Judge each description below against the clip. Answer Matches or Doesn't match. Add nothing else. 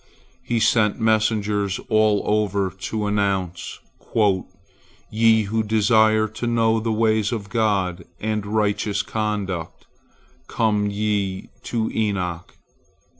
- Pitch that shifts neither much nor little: Doesn't match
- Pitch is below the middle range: Matches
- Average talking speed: Doesn't match